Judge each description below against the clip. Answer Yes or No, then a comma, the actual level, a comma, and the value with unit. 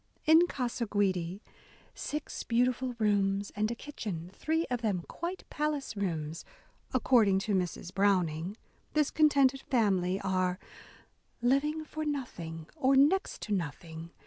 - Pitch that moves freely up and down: Yes, wide, 7.0 semitones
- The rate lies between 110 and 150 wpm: Yes, slow, 135 wpm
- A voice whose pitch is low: No, high, 215 Hz